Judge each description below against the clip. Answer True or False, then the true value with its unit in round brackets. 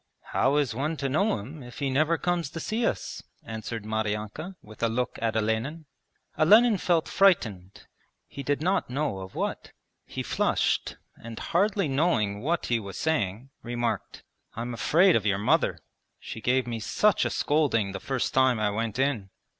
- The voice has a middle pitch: False (130 Hz)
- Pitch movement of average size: False (6.3 semitones)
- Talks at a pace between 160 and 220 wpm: True (170 wpm)